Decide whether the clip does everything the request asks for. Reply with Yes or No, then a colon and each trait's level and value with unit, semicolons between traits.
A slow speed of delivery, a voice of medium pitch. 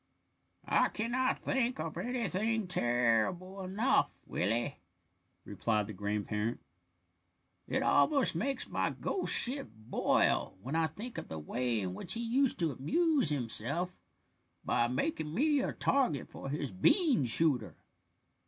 Yes: slow, 130 wpm; medium, 160 Hz